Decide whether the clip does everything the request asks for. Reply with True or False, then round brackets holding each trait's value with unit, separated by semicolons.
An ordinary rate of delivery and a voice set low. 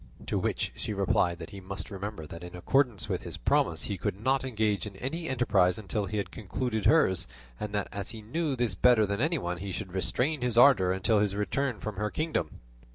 False (215 wpm; 105 Hz)